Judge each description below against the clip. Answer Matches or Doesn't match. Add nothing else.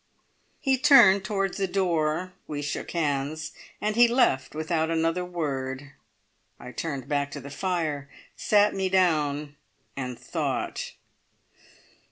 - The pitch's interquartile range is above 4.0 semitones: Matches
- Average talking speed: Doesn't match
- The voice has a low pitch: Doesn't match